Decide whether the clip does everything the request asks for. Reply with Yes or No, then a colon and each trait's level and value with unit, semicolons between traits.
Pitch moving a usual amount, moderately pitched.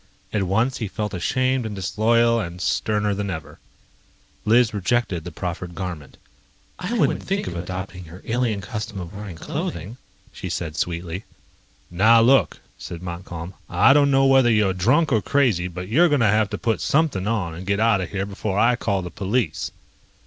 No: average, 4.5 semitones; low, 100 Hz